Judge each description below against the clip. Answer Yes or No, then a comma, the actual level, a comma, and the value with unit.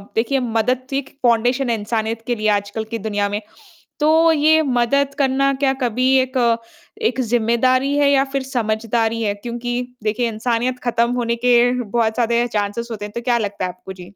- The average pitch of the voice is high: Yes, high, 235 Hz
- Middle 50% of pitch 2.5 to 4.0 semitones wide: Yes, average, 2.9 semitones